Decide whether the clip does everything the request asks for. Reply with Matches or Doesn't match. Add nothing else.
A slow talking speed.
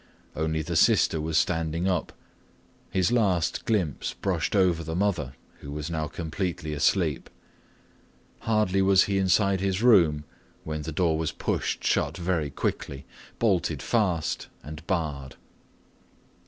Matches